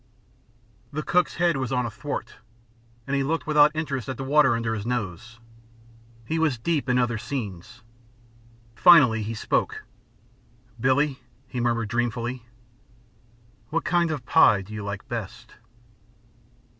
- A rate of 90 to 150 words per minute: Yes, average, 140 wpm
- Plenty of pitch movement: No, average, 4.6 semitones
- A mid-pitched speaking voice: No, low, 125 Hz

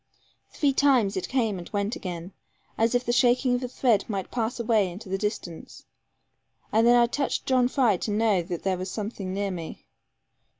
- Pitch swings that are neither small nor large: Yes, average, 4.2 semitones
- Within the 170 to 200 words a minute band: Yes, average, 185 wpm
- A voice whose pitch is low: No, high, 220 Hz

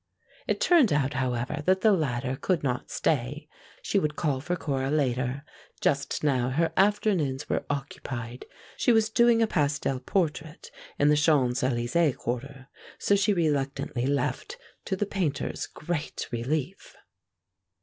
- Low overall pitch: No, medium, 145 Hz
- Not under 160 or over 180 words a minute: No, average, 140 wpm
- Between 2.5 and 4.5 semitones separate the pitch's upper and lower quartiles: No, average, 5.1 semitones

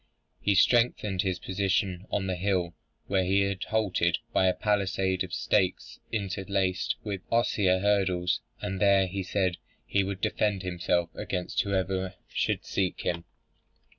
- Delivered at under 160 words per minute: Yes, average, 140 wpm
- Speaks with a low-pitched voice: Yes, very low, 95 Hz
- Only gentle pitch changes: Yes, narrow, 1.4 semitones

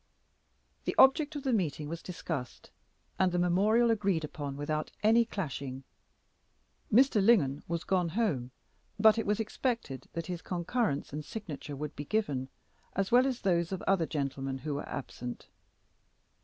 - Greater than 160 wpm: No, average, 155 wpm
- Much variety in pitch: Yes, wide, 7.0 semitones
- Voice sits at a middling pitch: Yes, medium, 175 Hz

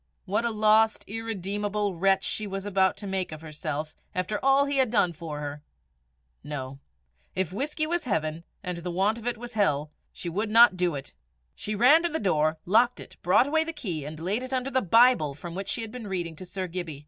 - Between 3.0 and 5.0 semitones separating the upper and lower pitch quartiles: No, wide, 5.5 semitones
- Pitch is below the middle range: No, high, 195 Hz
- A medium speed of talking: No, fast, 220 wpm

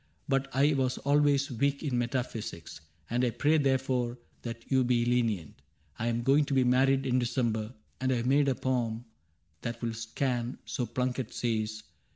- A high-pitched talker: No, low, 125 Hz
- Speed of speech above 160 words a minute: Yes, average, 180 wpm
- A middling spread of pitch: No, narrow, 2.3 semitones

